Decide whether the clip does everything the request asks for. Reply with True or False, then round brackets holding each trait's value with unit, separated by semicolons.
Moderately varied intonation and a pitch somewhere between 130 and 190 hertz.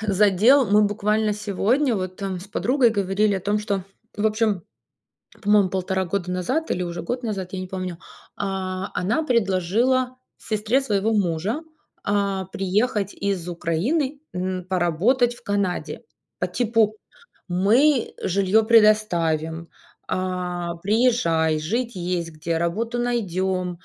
False (3.5 semitones; 200 Hz)